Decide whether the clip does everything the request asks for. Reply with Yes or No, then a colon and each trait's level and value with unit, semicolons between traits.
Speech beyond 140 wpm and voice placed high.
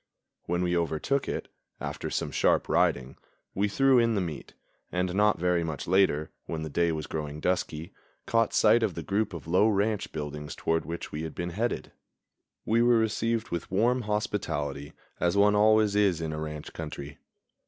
No: average, 180 wpm; very low, 90 Hz